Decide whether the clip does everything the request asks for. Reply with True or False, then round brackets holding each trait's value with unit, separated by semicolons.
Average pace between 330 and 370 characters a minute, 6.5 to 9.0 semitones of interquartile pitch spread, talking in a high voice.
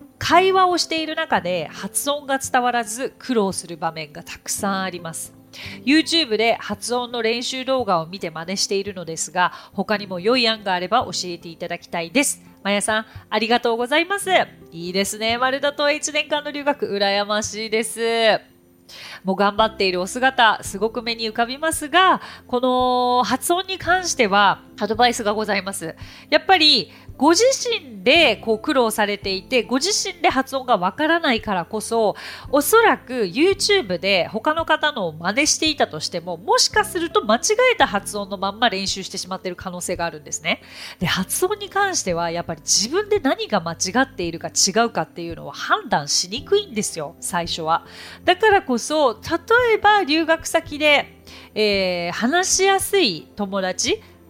True (350 characters per minute; 8.2 semitones; 230 Hz)